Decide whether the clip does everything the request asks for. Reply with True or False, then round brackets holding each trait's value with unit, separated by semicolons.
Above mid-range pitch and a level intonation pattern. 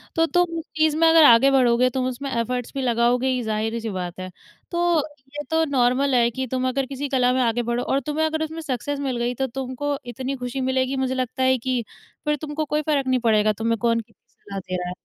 False (255 Hz; 3.1 semitones)